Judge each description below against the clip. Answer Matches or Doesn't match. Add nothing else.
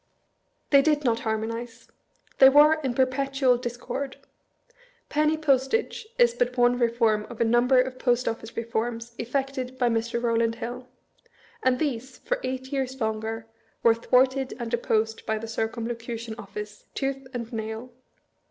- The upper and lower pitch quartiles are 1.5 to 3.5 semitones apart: Matches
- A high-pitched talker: Matches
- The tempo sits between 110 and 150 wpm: Matches